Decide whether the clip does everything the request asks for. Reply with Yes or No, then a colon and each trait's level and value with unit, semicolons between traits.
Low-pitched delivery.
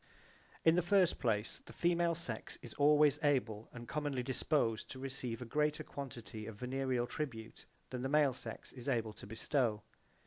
Yes: low, 130 Hz